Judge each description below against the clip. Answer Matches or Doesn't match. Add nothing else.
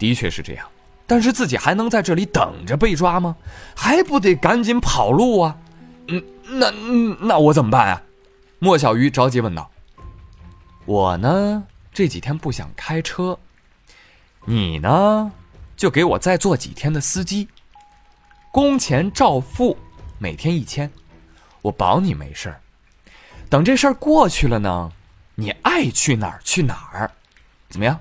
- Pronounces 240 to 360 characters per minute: Doesn't match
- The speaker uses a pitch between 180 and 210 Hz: Doesn't match